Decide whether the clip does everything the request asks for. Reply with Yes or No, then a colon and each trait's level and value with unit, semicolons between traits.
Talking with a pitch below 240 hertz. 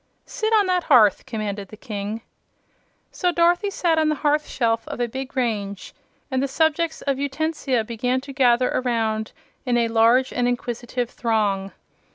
No: very high, 250 Hz